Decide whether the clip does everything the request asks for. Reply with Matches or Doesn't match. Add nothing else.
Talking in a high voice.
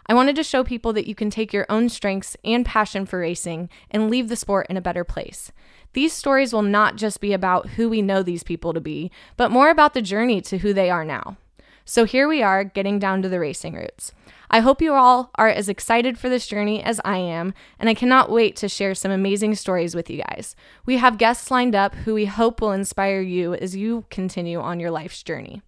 Matches